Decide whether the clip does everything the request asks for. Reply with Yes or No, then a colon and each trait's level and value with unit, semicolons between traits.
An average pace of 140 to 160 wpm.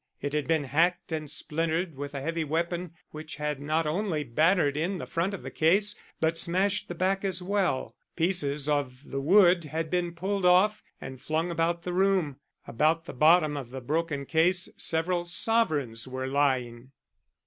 No: average, 175 wpm